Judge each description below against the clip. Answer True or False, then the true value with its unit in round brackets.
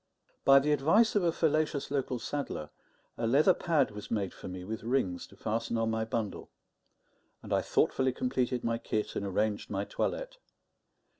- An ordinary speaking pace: True (170 wpm)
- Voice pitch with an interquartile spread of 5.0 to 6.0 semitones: True (5.3 semitones)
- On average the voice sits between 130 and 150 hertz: False (120 Hz)